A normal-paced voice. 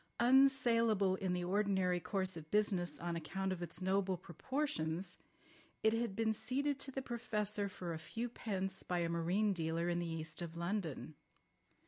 Yes: average, 165 wpm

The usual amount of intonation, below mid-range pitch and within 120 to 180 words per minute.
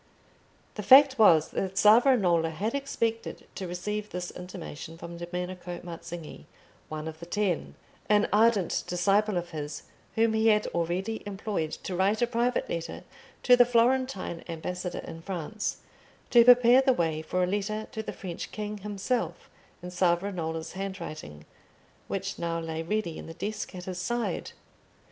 No: average, 4.1 semitones; high, 190 Hz; average, 155 wpm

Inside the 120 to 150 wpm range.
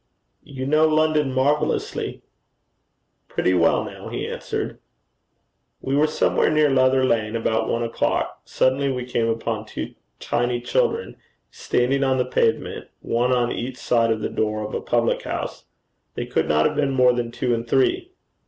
No: average, 160 wpm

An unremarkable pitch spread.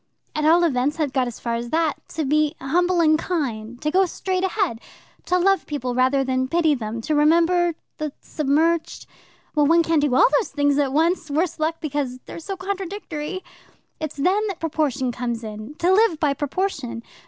Yes: average, 4.3 semitones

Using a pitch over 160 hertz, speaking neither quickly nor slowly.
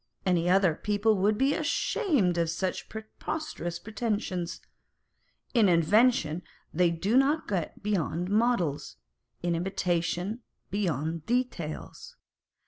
No: high, 190 Hz; slow, 105 wpm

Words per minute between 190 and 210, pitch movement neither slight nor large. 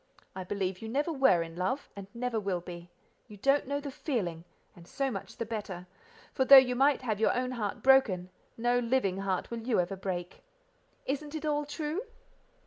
No: average, 195 wpm; wide, 6.2 semitones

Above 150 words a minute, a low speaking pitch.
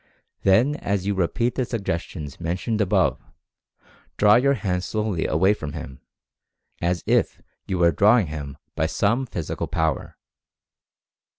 No: slow, 135 wpm; very low, 95 Hz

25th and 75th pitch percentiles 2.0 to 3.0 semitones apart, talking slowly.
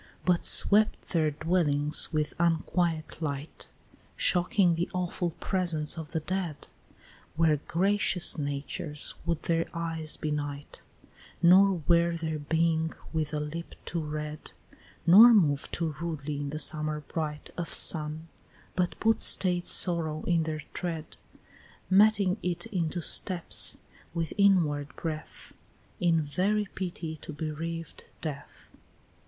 Yes: narrow, 2.6 semitones; slow, 125 wpm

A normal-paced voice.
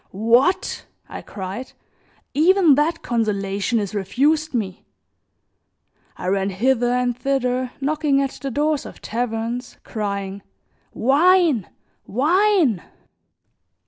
No: slow, 100 wpm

